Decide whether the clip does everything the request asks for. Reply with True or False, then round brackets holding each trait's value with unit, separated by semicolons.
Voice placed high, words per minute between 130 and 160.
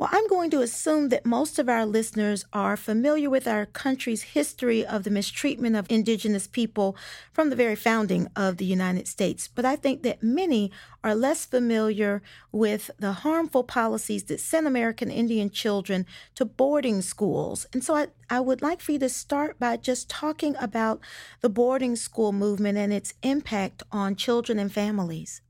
False (230 Hz; 175 wpm)